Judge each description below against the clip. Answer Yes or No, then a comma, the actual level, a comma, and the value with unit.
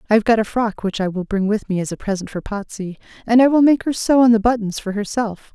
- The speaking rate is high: Yes, fast, 290 wpm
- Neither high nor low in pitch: No, high, 215 Hz